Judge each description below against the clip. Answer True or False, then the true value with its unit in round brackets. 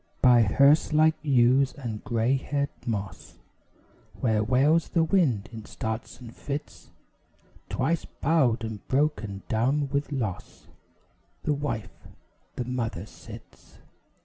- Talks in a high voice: False (125 Hz)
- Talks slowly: True (120 wpm)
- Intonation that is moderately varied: True (4.6 semitones)